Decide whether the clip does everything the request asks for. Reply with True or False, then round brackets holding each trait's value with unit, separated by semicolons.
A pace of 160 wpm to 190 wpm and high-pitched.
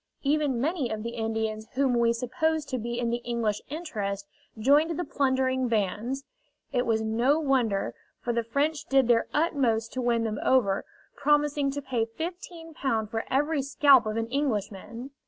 True (165 wpm; 250 Hz)